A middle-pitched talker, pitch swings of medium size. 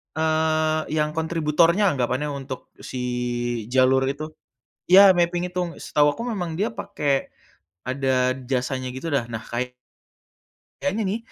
Yes: medium, 150 Hz; average, 4.6 semitones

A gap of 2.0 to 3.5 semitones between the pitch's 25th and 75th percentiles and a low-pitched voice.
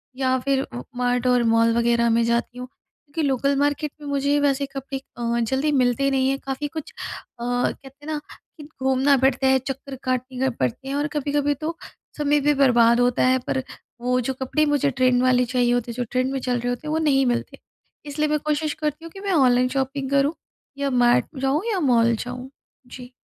No: narrow, 2.5 semitones; very high, 265 Hz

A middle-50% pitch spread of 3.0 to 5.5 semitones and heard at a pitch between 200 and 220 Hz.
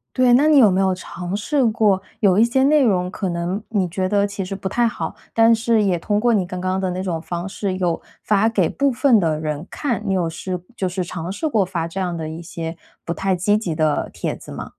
No: average, 3.8 semitones; high, 190 Hz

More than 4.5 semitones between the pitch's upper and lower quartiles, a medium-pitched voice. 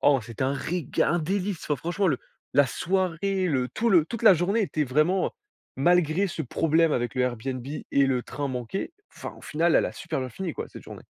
Yes: wide, 5.5 semitones; medium, 155 Hz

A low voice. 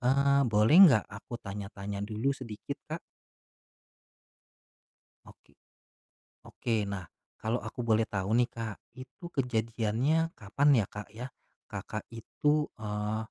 Yes: low, 110 Hz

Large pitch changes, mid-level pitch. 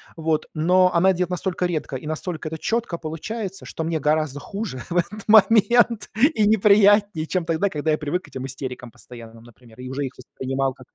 Yes: wide, 6.0 semitones; medium, 165 Hz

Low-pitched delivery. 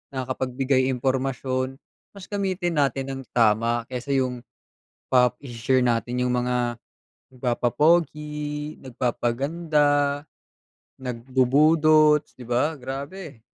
Yes: low, 130 Hz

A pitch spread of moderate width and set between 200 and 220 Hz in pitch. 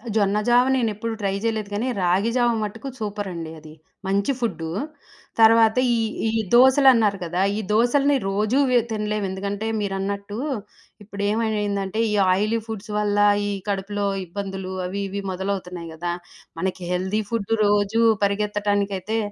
No: narrow, 2.3 semitones; high, 205 Hz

